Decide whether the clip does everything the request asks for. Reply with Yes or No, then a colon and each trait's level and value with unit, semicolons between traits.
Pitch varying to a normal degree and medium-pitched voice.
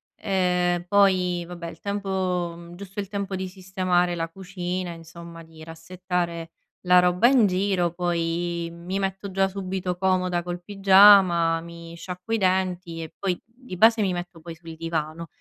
No: narrow, 2.1 semitones; medium, 180 Hz